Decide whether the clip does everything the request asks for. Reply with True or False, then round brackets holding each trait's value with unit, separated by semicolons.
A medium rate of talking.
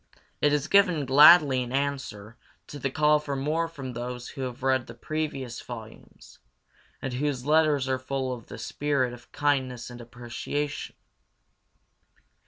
True (150 wpm)